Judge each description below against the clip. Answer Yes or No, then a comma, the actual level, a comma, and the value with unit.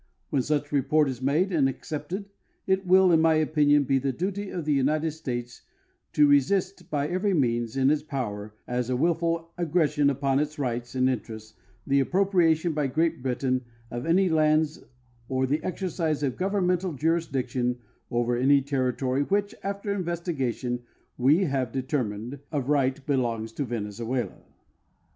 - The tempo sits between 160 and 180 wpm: No, average, 150 wpm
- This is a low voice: No, medium, 145 Hz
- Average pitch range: Yes, average, 4.5 semitones